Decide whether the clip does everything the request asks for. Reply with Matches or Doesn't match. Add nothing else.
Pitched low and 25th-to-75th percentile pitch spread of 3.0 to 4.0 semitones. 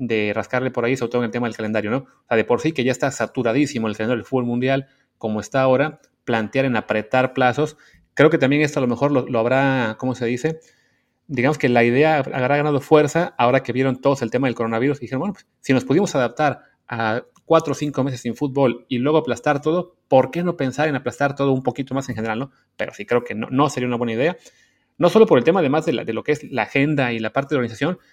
Matches